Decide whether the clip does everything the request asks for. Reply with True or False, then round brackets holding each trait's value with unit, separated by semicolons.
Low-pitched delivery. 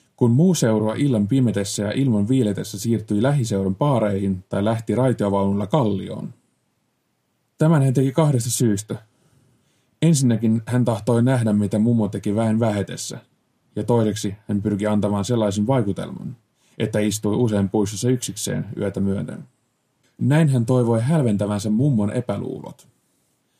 True (115 Hz)